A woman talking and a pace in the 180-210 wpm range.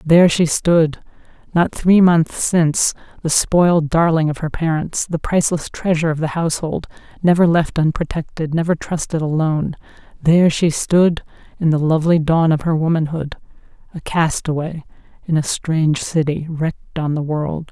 No: female; average, 145 wpm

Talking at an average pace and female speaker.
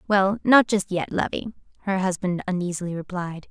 Yes: average, 155 wpm; female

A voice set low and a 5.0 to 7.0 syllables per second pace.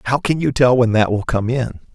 Yes: low, 120 Hz; 5.5 syllables/s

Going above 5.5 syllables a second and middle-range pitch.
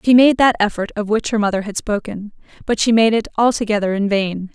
No: 5.8 syllables/s; high, 215 Hz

